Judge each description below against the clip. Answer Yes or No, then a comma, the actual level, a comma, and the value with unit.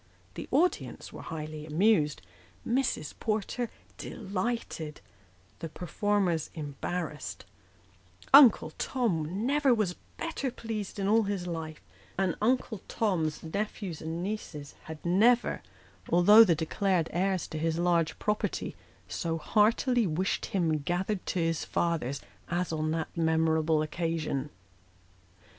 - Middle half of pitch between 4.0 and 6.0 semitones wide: Yes, average, 4.9 semitones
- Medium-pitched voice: Yes, medium, 175 Hz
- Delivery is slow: Yes, slow, 115 wpm